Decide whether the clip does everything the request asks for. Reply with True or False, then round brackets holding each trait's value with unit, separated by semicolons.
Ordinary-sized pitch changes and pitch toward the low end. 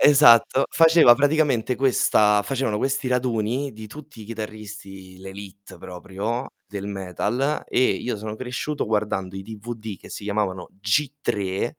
True (4.4 semitones; 110 Hz)